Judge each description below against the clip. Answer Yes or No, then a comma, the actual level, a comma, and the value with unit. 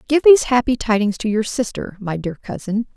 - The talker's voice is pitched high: Yes, high, 225 Hz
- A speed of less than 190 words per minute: No, fast, 205 wpm